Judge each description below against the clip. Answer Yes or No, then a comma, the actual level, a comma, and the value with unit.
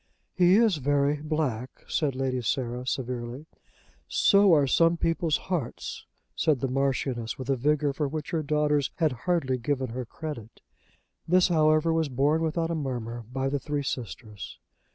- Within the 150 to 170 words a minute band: Yes, average, 155 wpm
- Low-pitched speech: No, medium, 145 Hz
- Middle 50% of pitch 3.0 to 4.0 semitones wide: Yes, average, 3.7 semitones